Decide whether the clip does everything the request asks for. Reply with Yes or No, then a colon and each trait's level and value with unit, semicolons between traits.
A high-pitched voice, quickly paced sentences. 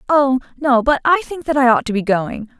Yes: very high, 260 Hz; fast, 255 wpm